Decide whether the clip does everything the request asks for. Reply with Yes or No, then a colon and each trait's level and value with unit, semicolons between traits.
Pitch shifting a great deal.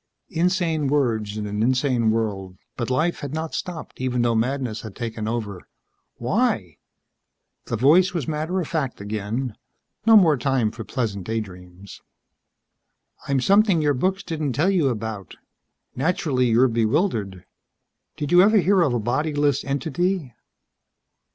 Yes: wide, 6.2 semitones